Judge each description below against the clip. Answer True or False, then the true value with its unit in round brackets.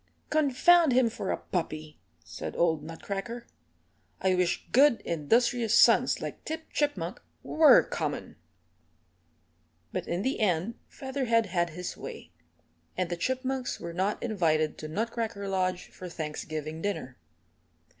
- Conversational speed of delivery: False (125 wpm)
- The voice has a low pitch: False (195 Hz)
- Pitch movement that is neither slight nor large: False (6.4 semitones)